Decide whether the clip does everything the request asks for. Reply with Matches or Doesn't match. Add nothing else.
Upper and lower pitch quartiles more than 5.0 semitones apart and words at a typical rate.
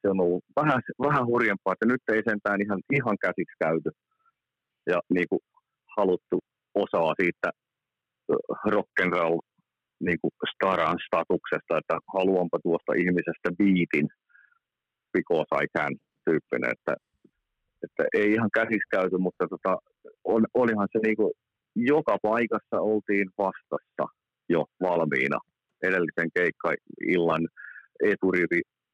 Doesn't match